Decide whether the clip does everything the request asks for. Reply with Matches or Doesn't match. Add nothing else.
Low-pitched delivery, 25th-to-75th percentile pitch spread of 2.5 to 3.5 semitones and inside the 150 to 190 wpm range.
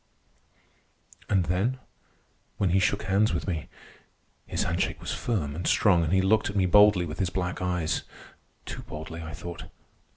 Matches